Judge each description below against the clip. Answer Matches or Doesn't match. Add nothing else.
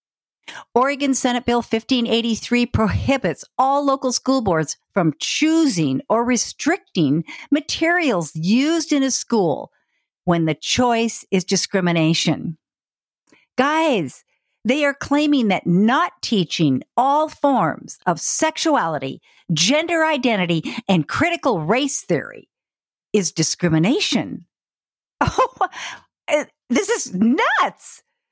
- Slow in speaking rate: Matches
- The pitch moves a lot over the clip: Matches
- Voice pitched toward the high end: Matches